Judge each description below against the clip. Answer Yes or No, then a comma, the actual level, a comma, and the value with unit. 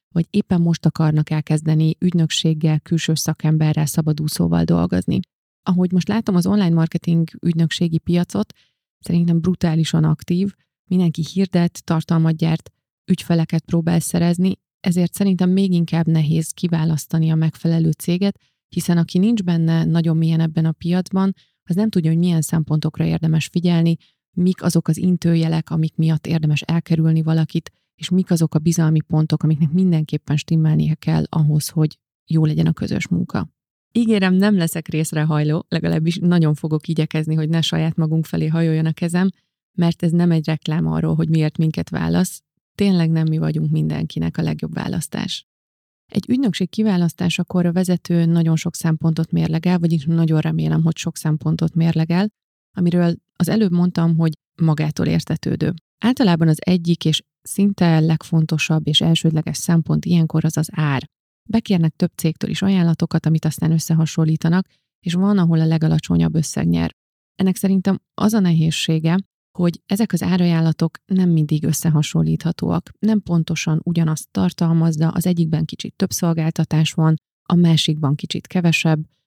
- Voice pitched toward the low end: No, medium, 165 Hz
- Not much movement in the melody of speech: Yes, narrow, 1.9 semitones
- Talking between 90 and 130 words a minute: No, average, 145 wpm